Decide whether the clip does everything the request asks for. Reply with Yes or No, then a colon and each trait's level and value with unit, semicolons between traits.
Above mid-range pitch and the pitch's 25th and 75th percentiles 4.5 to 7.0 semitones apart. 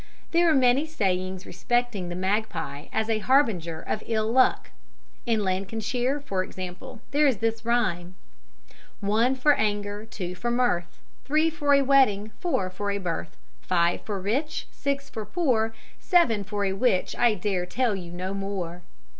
Yes: high, 215 Hz; average, 5.2 semitones